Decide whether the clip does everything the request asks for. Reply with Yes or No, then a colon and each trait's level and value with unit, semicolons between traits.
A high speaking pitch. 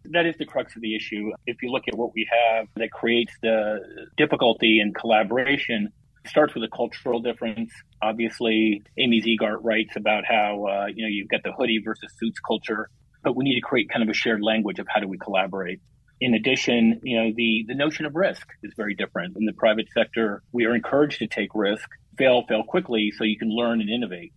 No: low, 115 Hz